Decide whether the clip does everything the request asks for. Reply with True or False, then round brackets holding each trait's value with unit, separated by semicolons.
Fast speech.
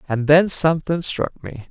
False (175 wpm)